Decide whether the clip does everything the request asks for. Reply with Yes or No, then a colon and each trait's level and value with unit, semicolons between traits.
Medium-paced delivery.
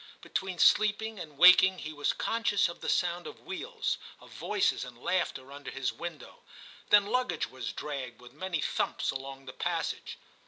Yes: average, 170 wpm